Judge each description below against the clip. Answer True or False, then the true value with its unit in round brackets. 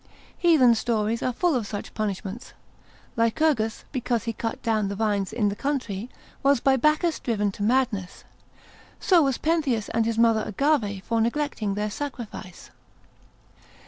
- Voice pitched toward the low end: False (230 Hz)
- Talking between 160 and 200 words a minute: False (145 wpm)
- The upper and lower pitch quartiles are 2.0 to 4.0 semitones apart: False (4.5 semitones)